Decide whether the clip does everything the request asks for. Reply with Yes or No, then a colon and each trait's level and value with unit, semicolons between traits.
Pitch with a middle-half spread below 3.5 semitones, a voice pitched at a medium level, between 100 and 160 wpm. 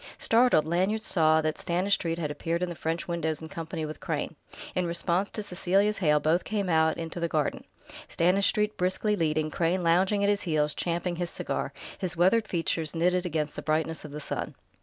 No: average, 2.8 semitones; medium, 170 Hz; average, 190 wpm